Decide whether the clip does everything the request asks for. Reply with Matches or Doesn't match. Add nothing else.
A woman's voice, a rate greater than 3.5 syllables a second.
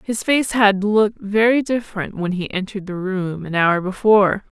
Matches